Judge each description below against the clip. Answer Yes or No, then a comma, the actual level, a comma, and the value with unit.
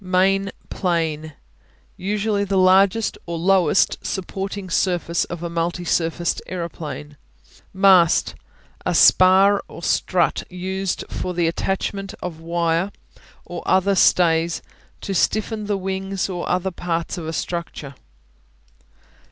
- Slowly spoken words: Yes, slow, 120 wpm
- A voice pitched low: No, medium, 185 Hz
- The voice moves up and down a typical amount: No, narrow, 2.3 semitones